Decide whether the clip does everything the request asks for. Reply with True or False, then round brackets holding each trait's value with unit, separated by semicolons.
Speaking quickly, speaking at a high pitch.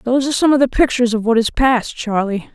True (260 wpm; 245 Hz)